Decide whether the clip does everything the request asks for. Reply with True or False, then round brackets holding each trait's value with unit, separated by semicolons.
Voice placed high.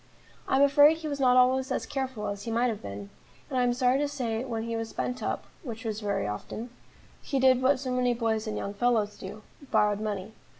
True (240 Hz)